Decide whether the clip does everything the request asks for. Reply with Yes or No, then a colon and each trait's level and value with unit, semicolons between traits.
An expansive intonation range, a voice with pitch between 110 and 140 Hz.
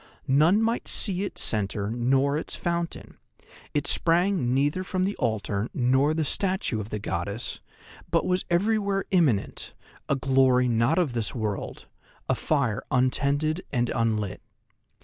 Yes: wide, 7.1 semitones; low, 135 Hz